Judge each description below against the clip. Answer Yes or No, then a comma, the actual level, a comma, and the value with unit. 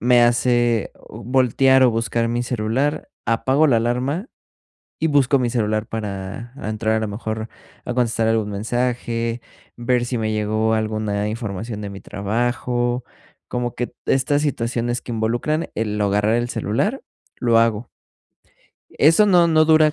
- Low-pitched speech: Yes, low, 120 Hz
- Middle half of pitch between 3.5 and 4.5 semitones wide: No, narrow, 2.5 semitones